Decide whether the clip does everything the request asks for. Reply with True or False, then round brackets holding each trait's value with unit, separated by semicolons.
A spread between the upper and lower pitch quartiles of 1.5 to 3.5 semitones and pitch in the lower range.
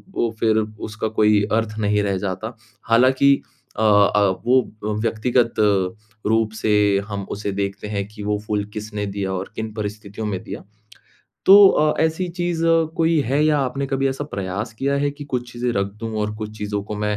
False (4.2 semitones; 110 Hz)